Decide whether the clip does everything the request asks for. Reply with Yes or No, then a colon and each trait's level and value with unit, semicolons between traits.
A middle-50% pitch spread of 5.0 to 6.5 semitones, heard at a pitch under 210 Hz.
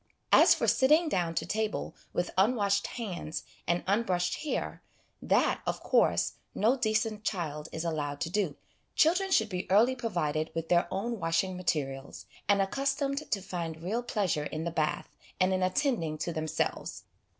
Yes: wide, 5.5 semitones; high, 190 Hz